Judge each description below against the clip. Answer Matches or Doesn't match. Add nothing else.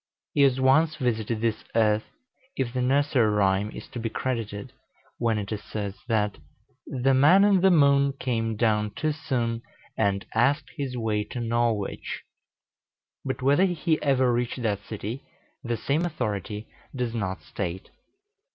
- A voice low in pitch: Matches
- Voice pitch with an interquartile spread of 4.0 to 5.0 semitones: Matches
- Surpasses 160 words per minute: Doesn't match